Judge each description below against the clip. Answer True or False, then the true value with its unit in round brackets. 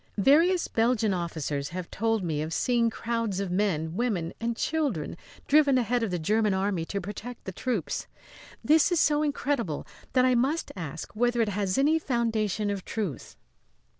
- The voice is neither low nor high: False (220 Hz)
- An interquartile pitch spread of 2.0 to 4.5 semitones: False (5.3 semitones)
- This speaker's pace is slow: False (165 wpm)